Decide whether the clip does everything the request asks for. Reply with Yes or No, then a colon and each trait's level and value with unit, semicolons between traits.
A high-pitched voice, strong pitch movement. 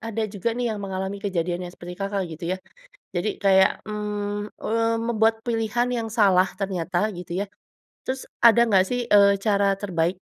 No: high, 205 Hz; average, 3.0 semitones